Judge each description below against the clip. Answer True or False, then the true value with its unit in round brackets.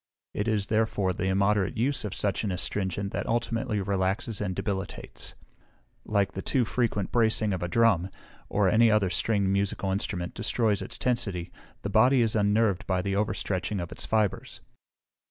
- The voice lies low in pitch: True (100 Hz)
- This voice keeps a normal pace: True (165 wpm)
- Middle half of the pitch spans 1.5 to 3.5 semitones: True (2.6 semitones)